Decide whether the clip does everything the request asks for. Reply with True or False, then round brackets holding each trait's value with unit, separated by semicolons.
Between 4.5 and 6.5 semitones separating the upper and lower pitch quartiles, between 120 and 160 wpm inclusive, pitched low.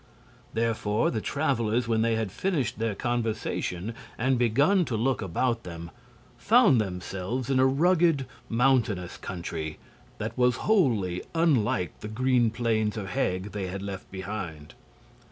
True (4.9 semitones; 135 wpm; 115 Hz)